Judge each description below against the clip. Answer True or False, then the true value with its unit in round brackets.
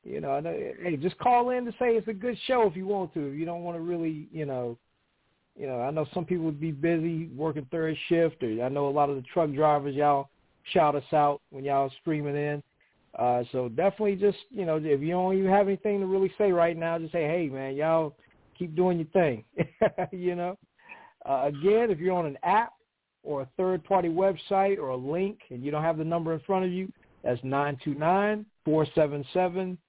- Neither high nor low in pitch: True (170 Hz)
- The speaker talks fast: True (220 wpm)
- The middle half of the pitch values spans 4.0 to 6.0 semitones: True (4.6 semitones)